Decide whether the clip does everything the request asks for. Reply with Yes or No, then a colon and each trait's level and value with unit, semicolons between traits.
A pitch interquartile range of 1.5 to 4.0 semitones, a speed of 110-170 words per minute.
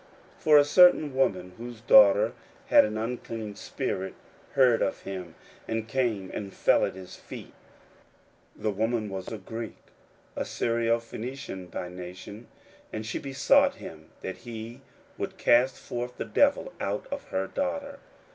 No: average, 5.0 semitones; average, 155 wpm